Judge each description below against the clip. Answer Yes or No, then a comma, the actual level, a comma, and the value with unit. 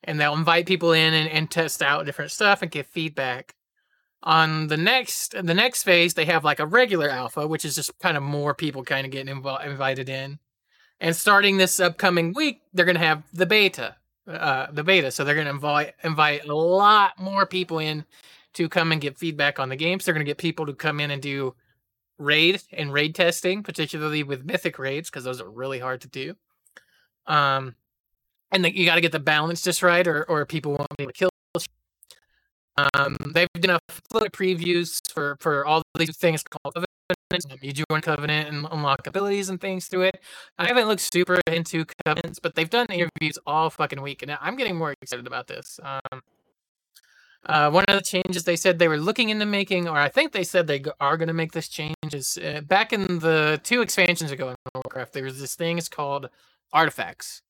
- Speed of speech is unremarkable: No, fast, 215 wpm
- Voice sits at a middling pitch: Yes, medium, 160 Hz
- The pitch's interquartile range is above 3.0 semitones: Yes, average, 3.9 semitones